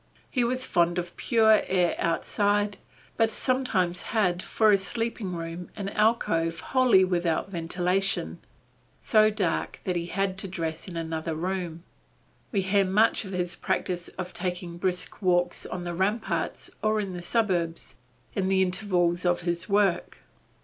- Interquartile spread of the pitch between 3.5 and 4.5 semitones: No, average, 2.9 semitones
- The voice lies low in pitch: No, medium, 185 Hz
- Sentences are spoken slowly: No, average, 150 wpm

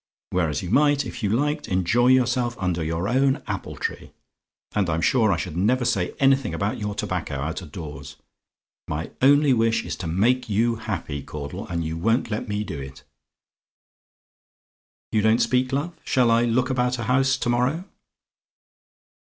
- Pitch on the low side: Yes, low, 110 Hz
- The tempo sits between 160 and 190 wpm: Yes, average, 170 wpm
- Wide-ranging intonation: Yes, wide, 6.2 semitones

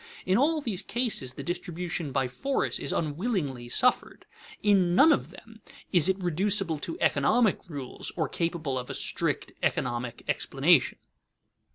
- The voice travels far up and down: Yes, wide, 6.6 semitones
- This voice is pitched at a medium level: Yes, medium, 175 Hz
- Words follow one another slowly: No, average, 145 wpm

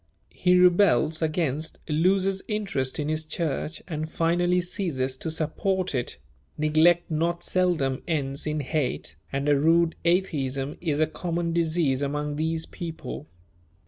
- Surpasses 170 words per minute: No, slow, 135 wpm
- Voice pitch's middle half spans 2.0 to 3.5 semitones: Yes, average, 2.8 semitones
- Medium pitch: Yes, medium, 160 Hz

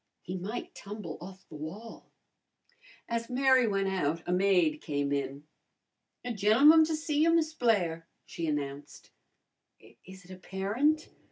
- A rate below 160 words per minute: Yes, average, 145 wpm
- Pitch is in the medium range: No, high, 195 Hz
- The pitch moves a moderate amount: No, wide, 6.8 semitones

